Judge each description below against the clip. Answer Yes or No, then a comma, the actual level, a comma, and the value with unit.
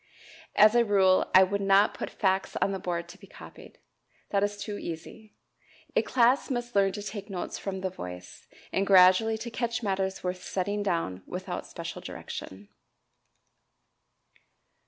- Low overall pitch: No, high, 195 Hz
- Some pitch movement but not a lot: No, narrow, 2.2 semitones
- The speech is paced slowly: No, average, 155 wpm